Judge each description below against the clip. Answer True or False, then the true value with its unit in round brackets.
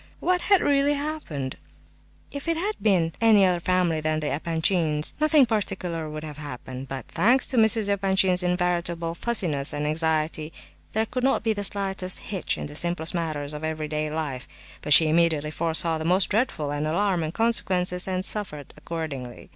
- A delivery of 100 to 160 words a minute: False (170 wpm)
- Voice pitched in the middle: True (170 Hz)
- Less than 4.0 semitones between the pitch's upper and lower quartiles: False (4.7 semitones)